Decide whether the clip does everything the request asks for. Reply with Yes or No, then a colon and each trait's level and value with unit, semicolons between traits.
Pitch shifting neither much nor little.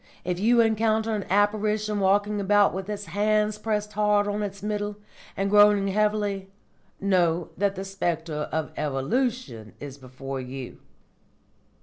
Yes: average, 3.3 semitones